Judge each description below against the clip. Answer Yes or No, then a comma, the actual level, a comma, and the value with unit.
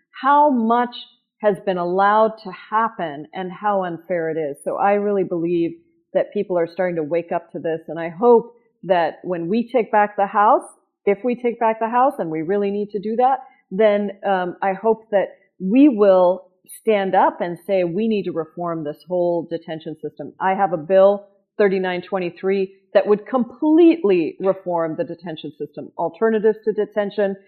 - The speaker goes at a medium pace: Yes, average, 180 wpm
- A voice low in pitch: No, high, 195 Hz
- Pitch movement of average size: Yes, average, 4.1 semitones